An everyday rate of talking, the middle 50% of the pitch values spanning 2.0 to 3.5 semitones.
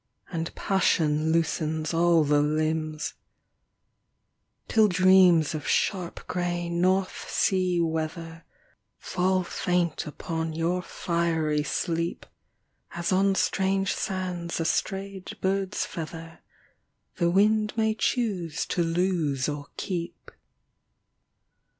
No: slow, 100 wpm; narrow, 2.6 semitones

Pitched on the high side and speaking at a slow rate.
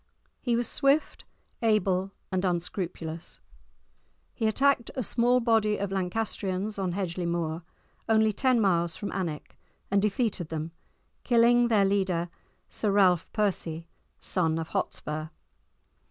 Yes: high, 195 Hz; slow, 125 wpm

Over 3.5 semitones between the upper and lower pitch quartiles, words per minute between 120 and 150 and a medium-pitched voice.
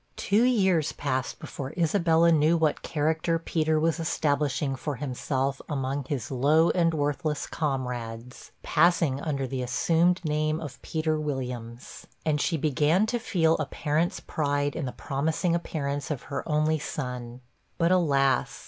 No: average, 3.2 semitones; average, 145 wpm; medium, 150 Hz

